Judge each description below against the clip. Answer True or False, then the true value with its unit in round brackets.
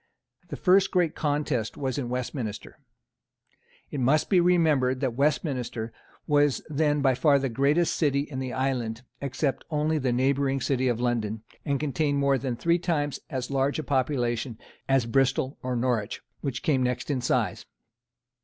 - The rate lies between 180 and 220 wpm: False (160 wpm)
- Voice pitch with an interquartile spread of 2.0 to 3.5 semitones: True (2.8 semitones)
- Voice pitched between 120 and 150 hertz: True (135 Hz)